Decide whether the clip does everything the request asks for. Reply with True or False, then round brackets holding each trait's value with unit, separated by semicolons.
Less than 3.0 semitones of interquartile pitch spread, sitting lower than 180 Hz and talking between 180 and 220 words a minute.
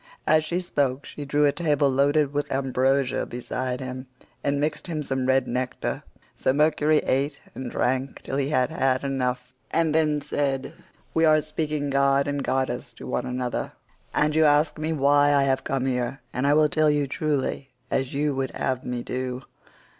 True (2.4 semitones; 140 Hz; 185 wpm)